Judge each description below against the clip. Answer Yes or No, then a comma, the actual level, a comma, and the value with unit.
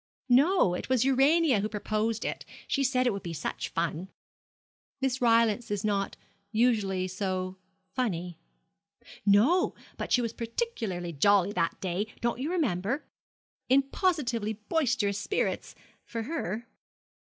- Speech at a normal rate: No, slow, 130 wpm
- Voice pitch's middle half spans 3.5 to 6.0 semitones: Yes, average, 5.1 semitones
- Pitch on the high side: Yes, high, 225 Hz